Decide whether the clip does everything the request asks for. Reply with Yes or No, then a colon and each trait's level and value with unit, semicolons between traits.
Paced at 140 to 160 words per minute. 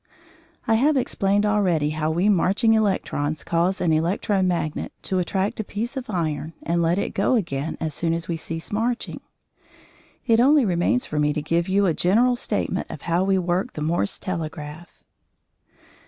No: average, 175 wpm